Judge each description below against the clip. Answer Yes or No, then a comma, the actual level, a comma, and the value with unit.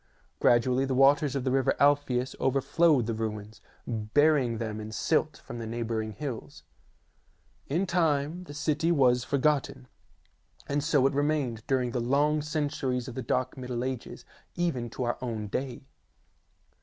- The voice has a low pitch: Yes, low, 130 Hz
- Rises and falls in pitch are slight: No, average, 3.6 semitones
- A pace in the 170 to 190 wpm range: No, average, 155 wpm